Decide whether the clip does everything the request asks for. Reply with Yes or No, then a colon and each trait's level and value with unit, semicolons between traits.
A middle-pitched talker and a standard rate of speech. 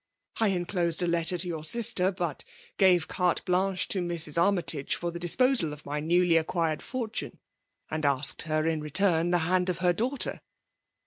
Yes: medium, 175 Hz; average, 185 wpm